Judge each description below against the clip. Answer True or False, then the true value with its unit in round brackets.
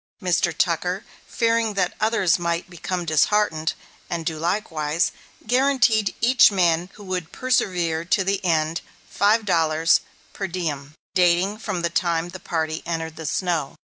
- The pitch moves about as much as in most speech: True (3.5 semitones)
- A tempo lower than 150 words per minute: True (140 wpm)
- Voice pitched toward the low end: False (175 Hz)